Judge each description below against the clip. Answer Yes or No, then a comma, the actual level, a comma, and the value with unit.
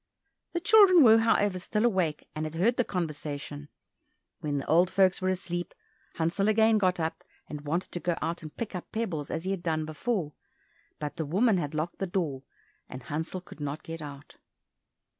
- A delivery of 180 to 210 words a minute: Yes, average, 190 wpm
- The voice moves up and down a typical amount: Yes, average, 4.4 semitones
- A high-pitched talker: No, medium, 175 Hz